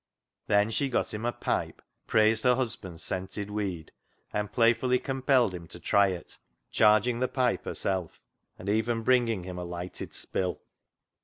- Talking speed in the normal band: Yes, average, 165 wpm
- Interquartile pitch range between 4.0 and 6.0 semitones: Yes, average, 4.4 semitones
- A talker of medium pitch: No, low, 105 Hz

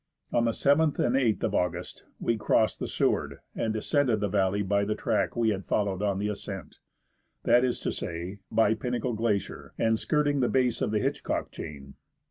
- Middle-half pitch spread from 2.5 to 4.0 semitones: Yes, average, 3.3 semitones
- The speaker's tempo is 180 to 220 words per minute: Yes, average, 190 wpm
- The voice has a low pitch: Yes, low, 110 Hz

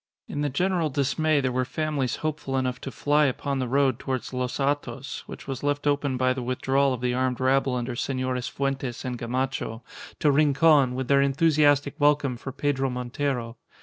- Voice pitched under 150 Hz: Yes, low, 135 Hz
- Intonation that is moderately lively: No, narrow, 2.2 semitones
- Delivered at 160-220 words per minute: Yes, average, 180 wpm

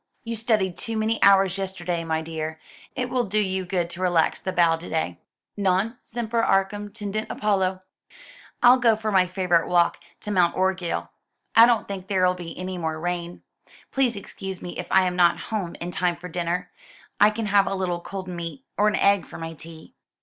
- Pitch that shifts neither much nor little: Yes, average, 3.2 semitones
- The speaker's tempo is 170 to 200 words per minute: Yes, average, 195 wpm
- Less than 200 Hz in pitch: Yes, medium, 185 Hz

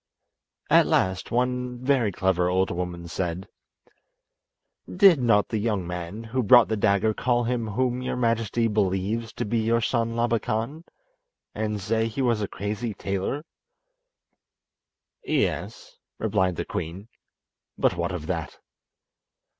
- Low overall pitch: Yes, low, 110 Hz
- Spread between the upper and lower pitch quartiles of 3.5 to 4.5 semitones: Yes, average, 4.0 semitones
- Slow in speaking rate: Yes, slow, 130 wpm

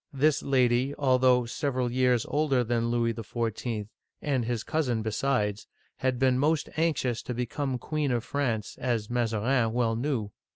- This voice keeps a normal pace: Yes, average, 155 wpm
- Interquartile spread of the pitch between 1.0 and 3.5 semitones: Yes, average, 2.8 semitones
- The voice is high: No, low, 125 Hz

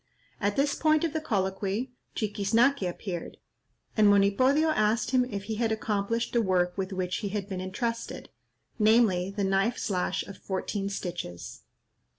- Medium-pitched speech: No, high, 205 Hz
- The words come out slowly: No, average, 150 wpm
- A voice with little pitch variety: No, average, 3.4 semitones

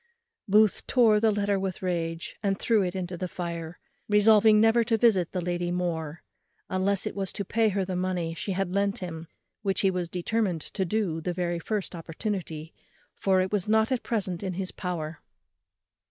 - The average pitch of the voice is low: No, medium, 185 Hz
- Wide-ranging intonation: No, average, 3.0 semitones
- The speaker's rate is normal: Yes, average, 185 wpm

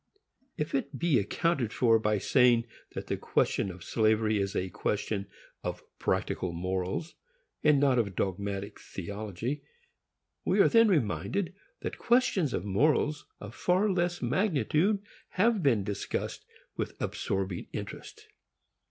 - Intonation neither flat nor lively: No, wide, 8.5 semitones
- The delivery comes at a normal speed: No, slow, 130 wpm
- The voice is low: Yes, low, 115 Hz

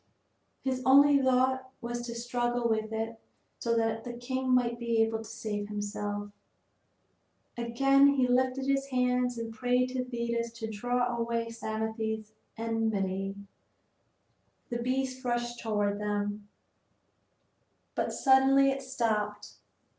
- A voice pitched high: Yes, high, 235 Hz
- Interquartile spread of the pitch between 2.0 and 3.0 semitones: Yes, narrow, 2.5 semitones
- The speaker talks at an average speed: No, slow, 125 wpm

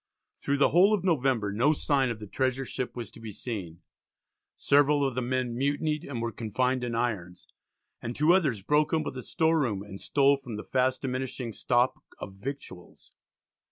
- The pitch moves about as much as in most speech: Yes, average, 3.8 semitones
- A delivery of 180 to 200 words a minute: Yes, average, 185 wpm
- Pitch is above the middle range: No, low, 130 Hz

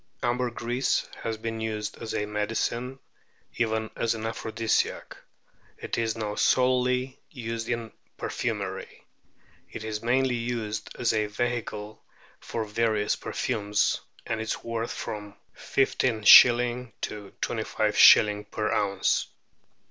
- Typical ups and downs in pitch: No, narrow, 2.1 semitones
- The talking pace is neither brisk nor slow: No, slow, 115 wpm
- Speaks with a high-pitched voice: No, low, 115 Hz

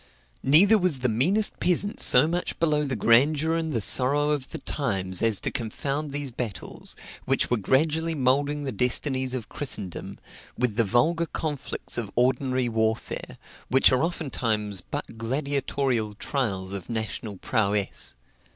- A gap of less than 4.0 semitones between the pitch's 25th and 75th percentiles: No, average, 4.8 semitones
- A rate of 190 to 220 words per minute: No, average, 145 wpm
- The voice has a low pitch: Yes, low, 130 Hz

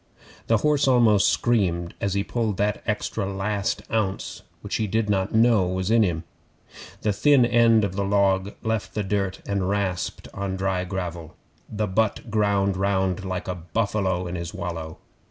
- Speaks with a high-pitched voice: No, low, 100 Hz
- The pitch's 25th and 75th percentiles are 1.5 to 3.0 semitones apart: Yes, narrow, 2.6 semitones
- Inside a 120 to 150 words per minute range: No, average, 170 wpm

